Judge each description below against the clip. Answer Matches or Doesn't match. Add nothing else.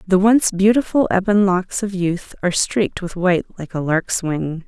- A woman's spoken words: Matches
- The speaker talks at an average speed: Matches